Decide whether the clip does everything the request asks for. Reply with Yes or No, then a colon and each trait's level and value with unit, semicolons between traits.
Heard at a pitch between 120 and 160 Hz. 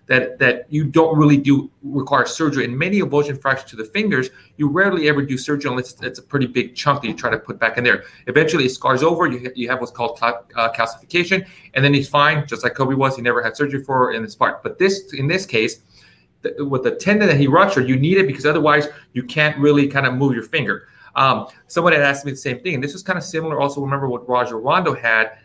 Yes: medium, 140 Hz